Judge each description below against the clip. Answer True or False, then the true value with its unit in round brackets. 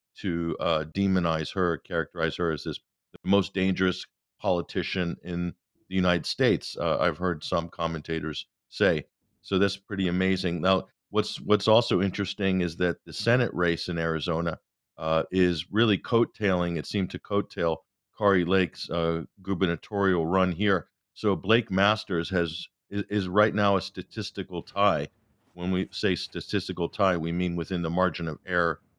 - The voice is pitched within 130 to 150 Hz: False (90 Hz)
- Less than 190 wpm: True (155 wpm)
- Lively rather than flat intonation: False (2.6 semitones)